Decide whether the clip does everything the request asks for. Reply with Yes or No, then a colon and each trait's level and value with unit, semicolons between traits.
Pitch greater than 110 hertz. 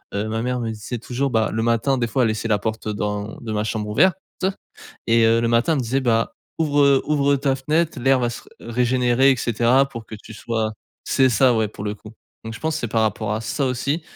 Yes: low, 120 Hz